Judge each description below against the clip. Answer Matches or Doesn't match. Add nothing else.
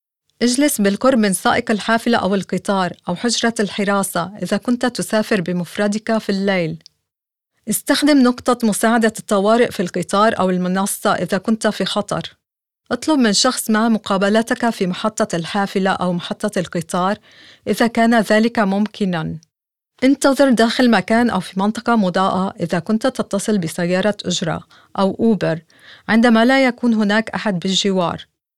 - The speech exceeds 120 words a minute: Matches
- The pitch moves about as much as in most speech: Matches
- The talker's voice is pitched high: Matches